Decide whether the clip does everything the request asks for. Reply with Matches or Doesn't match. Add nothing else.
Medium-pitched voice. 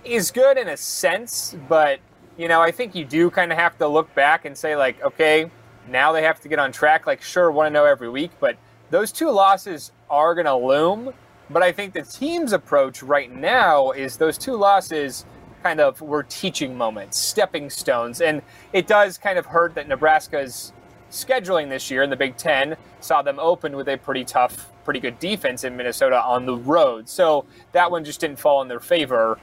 Matches